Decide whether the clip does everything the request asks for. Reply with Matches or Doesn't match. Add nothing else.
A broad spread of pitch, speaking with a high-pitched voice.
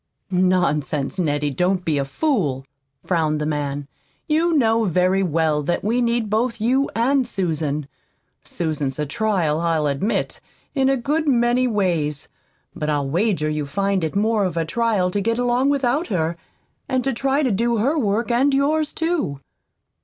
Matches